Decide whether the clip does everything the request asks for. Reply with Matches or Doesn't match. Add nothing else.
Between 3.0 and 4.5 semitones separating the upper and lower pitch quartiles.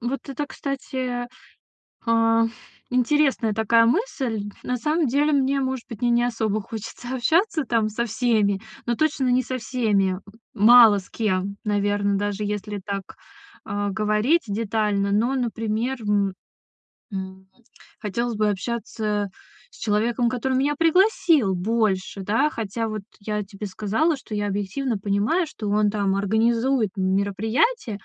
Matches